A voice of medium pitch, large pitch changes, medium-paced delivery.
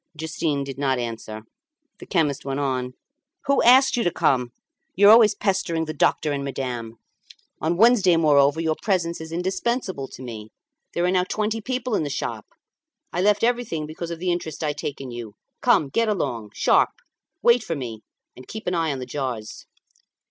Yes: medium, 160 Hz; wide, 6.5 semitones; average, 185 wpm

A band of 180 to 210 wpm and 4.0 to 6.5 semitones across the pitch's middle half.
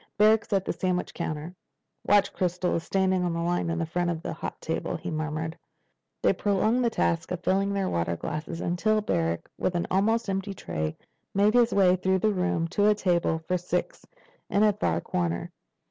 No: average, 190 wpm; average, 3.3 semitones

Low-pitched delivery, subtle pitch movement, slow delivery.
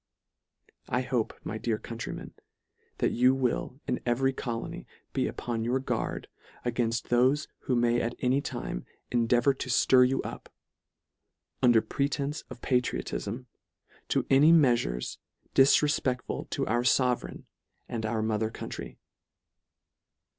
Yes: low, 125 Hz; narrow, 2.2 semitones; slow, 125 wpm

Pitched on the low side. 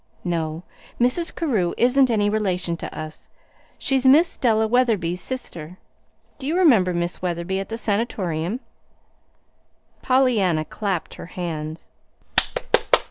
No: high, 200 Hz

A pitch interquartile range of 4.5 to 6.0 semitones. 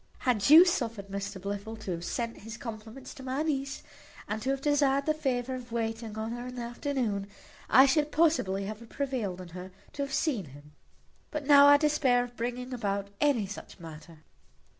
Yes: wide, 5.4 semitones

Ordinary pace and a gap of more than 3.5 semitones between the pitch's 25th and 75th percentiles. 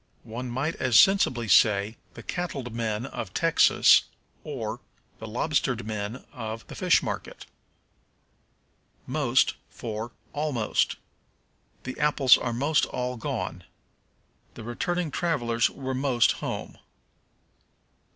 No: slow, 110 wpm; average, 4.1 semitones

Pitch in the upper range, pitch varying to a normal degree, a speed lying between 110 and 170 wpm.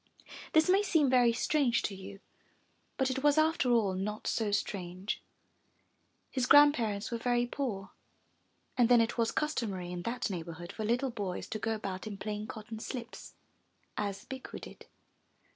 Yes: high, 225 Hz; average, 4.3 semitones; average, 160 wpm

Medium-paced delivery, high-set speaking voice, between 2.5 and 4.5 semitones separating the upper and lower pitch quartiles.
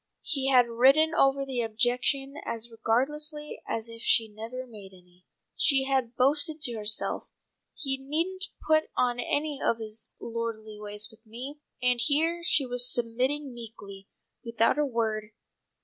Yes: average, 150 wpm; high, 245 Hz; average, 3.6 semitones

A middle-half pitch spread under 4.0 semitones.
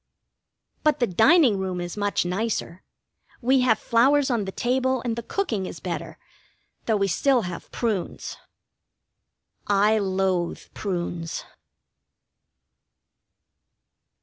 No: average, 5.0 semitones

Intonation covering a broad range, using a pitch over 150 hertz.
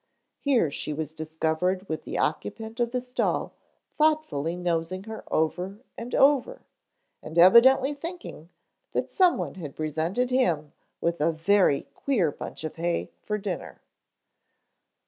Yes: wide, 7.7 semitones; medium, 185 Hz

